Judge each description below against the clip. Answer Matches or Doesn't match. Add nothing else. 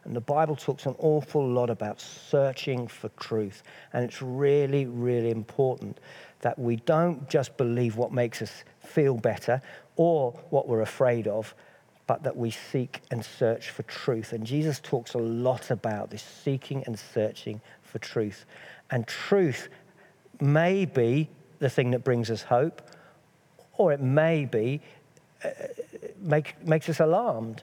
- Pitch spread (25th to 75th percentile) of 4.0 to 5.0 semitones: Matches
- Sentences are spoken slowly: Doesn't match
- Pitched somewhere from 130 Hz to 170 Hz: Matches